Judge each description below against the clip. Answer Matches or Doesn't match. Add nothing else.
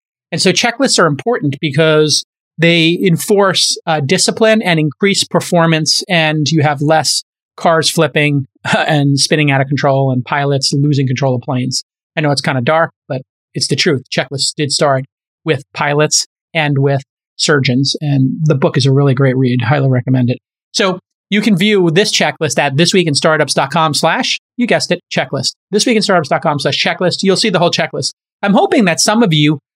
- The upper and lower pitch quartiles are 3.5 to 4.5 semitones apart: Matches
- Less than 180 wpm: Doesn't match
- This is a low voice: Doesn't match